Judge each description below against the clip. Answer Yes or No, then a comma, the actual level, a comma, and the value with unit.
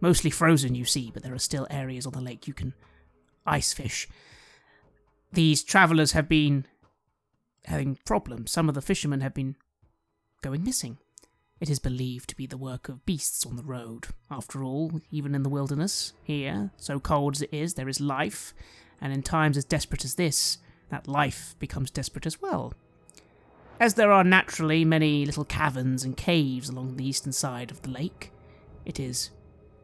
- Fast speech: No, average, 175 wpm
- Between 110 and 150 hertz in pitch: Yes, medium, 140 Hz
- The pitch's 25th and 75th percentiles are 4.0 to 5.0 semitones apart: No, average, 3.3 semitones